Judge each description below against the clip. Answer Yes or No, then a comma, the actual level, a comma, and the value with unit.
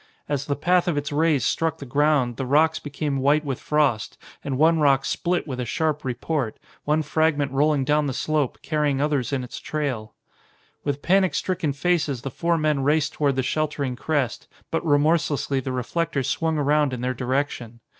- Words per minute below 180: No, average, 185 wpm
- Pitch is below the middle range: No, medium, 145 Hz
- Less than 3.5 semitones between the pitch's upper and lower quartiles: Yes, narrow, 2.5 semitones